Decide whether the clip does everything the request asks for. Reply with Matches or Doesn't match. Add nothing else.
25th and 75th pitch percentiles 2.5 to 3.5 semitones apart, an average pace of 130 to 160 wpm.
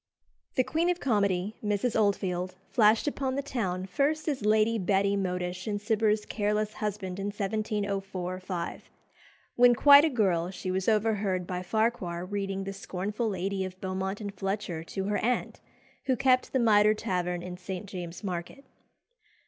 Matches